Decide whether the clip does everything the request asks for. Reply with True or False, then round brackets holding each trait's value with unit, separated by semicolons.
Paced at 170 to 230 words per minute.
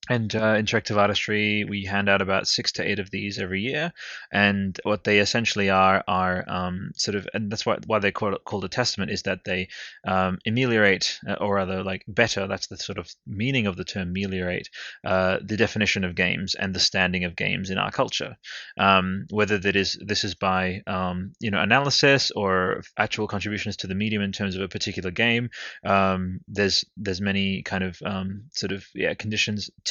True (200 wpm)